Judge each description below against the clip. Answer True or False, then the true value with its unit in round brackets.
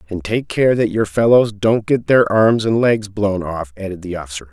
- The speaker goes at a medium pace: False (225 wpm)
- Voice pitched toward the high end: False (105 Hz)